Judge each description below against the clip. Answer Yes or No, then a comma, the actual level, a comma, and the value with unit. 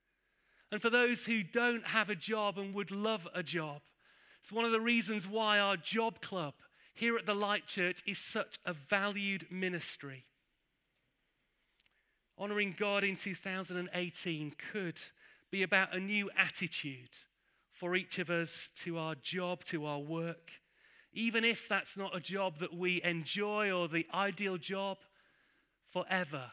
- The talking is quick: No, average, 150 wpm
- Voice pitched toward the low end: No, high, 195 Hz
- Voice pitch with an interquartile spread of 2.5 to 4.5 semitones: Yes, average, 3.2 semitones